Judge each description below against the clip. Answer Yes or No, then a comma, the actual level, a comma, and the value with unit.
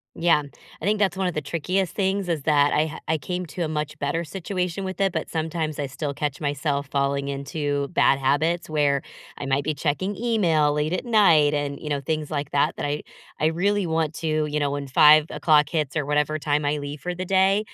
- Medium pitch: Yes, medium, 155 Hz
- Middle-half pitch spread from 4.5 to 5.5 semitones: No, average, 3.4 semitones